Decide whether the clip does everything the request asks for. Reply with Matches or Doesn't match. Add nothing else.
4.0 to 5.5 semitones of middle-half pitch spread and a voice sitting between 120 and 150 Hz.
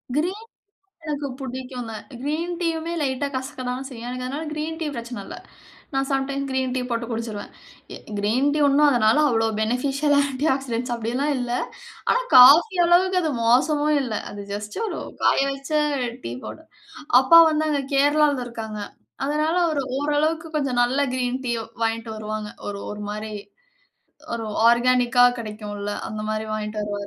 Doesn't match